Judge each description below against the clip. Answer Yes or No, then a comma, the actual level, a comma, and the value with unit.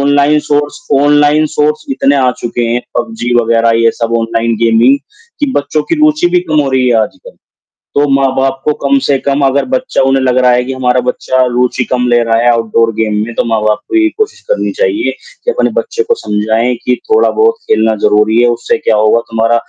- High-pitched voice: No, low, 130 Hz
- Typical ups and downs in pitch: Yes, average, 4.4 semitones